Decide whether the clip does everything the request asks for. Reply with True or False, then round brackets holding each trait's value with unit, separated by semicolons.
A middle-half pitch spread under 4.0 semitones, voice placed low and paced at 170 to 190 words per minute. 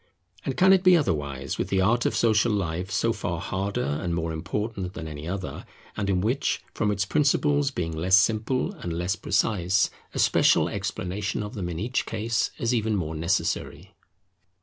False (4.7 semitones; 100 Hz; 180 wpm)